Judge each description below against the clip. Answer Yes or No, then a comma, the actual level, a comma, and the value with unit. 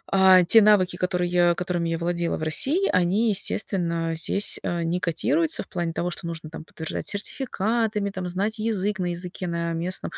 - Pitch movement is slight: No, average, 3.3 semitones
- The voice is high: No, medium, 180 Hz